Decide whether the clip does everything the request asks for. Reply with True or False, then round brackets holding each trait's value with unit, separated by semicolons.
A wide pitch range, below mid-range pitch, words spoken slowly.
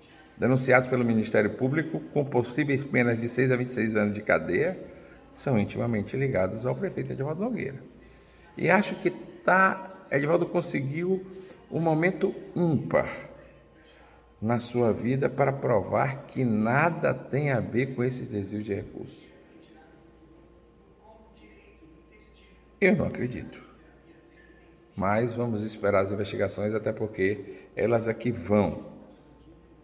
True (5.9 semitones; 125 Hz; 115 wpm)